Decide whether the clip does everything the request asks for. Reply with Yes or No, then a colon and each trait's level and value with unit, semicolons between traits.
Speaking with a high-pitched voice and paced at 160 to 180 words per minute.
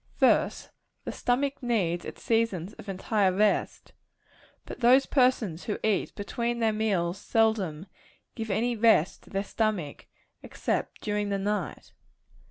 No: high, 210 Hz; slow, 135 wpm